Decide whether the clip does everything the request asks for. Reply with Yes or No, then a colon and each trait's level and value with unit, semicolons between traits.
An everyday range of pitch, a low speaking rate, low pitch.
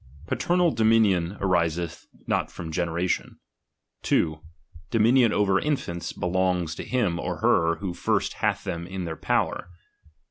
Yes: average, 4.1 semitones; slow, 130 wpm; very low, 90 Hz